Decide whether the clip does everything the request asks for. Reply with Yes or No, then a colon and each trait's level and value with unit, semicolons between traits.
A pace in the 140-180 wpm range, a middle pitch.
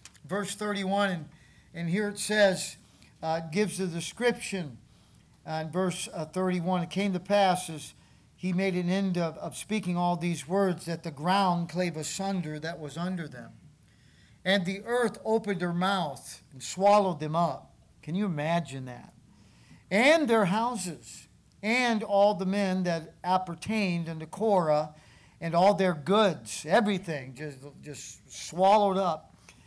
Yes: average, 150 wpm; medium, 180 Hz